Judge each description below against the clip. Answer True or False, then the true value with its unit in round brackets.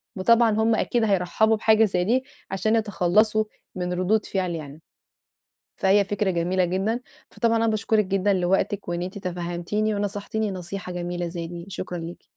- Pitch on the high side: True (195 Hz)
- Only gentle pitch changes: False (3.4 semitones)